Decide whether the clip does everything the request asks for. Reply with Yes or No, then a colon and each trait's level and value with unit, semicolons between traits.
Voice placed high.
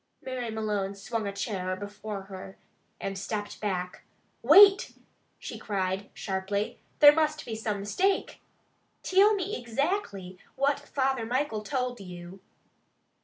Yes: high, 215 Hz